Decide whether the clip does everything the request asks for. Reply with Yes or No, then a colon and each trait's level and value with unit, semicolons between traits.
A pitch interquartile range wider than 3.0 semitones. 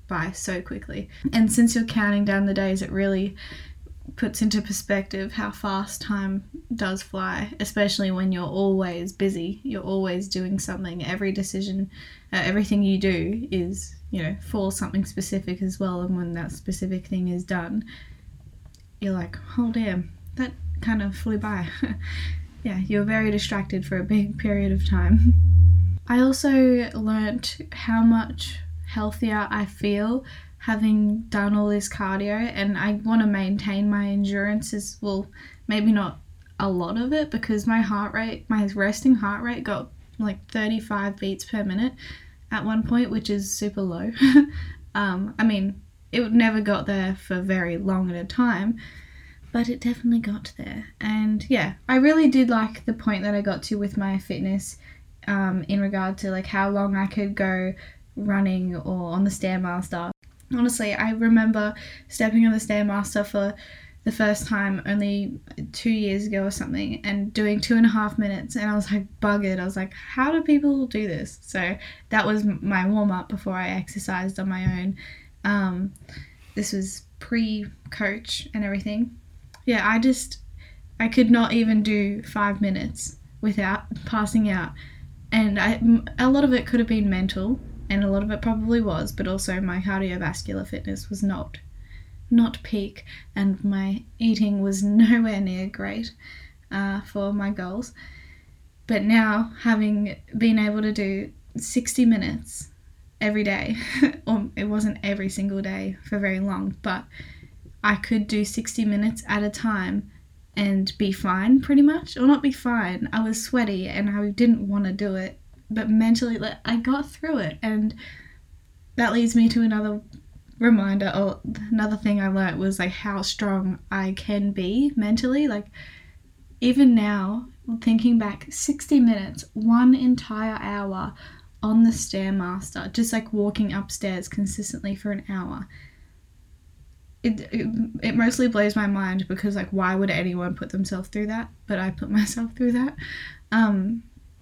No: average, 2.7 semitones